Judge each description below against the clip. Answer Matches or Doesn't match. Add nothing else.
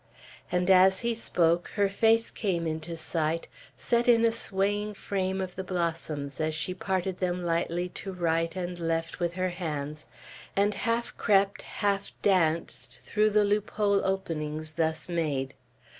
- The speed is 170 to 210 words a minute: Doesn't match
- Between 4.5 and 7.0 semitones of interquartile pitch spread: Doesn't match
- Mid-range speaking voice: Matches